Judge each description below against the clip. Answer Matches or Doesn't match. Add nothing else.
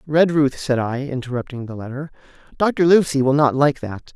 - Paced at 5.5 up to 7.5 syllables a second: Doesn't match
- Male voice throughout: Matches